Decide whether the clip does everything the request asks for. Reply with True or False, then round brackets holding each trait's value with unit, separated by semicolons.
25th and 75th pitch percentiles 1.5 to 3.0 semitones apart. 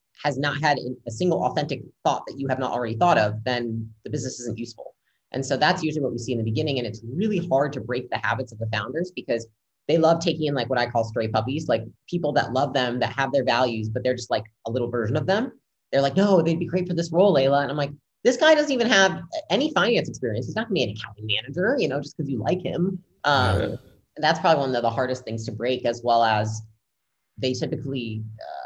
False (5.2 semitones)